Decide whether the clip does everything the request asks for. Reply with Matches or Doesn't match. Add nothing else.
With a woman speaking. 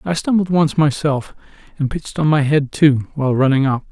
Doesn't match